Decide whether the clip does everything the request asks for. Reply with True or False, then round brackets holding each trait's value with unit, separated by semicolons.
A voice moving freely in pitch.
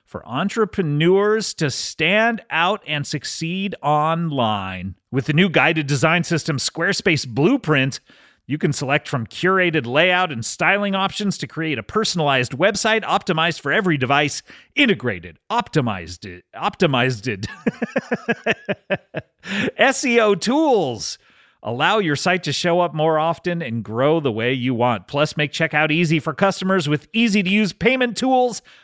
True (5.7 semitones)